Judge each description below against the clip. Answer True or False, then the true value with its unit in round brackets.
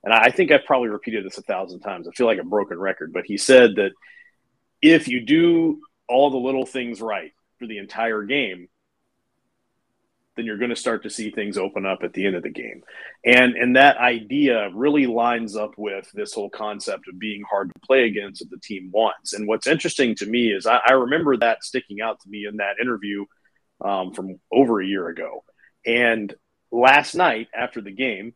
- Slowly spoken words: False (205 wpm)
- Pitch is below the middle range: True (115 Hz)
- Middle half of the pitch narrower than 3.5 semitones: False (4.2 semitones)